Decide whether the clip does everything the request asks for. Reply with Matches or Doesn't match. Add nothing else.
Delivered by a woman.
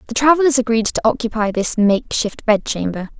Matches